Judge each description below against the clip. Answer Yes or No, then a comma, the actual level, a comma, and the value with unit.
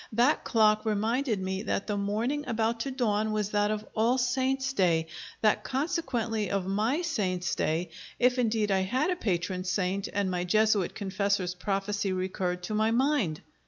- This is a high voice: Yes, high, 210 Hz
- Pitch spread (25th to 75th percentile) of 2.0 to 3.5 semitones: No, average, 4.0 semitones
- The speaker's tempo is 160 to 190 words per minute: Yes, average, 165 wpm